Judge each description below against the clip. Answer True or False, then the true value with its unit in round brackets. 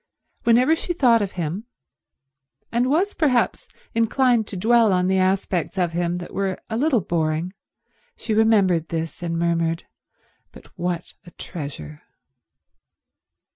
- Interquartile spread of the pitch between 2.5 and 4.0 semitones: False (5.4 semitones)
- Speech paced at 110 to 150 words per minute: True (135 wpm)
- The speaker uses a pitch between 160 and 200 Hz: True (190 Hz)